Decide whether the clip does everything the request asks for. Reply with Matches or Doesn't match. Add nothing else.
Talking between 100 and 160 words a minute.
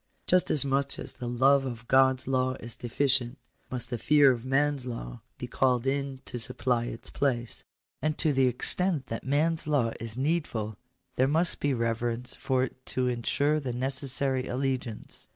Doesn't match